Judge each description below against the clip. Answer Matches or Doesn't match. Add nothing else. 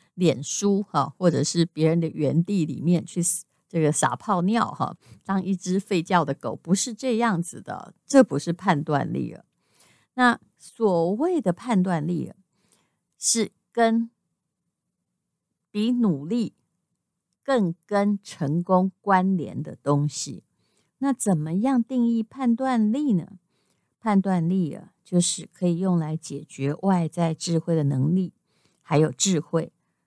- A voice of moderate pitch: Matches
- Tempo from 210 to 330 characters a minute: Doesn't match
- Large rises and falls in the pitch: Doesn't match